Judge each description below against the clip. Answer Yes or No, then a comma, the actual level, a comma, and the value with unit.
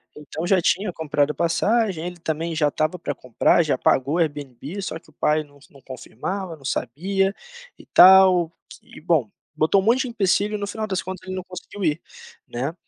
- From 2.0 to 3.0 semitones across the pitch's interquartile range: No, average, 4.3 semitones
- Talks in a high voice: No, medium, 170 Hz